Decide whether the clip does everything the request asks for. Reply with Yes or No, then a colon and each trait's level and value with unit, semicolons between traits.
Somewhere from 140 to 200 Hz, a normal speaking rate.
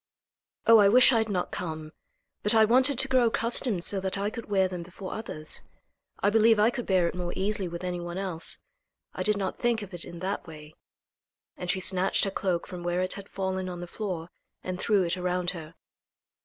No: high, 190 Hz; fast, 220 wpm